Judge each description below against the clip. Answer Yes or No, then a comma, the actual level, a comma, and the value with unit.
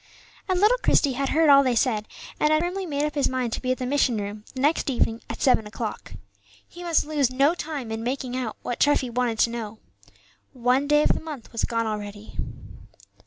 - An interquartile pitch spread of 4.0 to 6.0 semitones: Yes, average, 4.5 semitones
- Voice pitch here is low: No, very high, 255 Hz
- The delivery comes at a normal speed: No, fast, 215 wpm